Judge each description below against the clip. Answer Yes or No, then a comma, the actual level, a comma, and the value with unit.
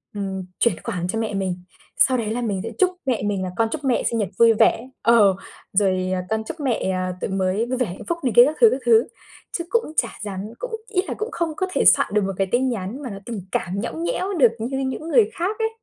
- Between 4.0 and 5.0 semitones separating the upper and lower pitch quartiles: No, wide, 5.4 semitones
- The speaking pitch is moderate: No, high, 230 Hz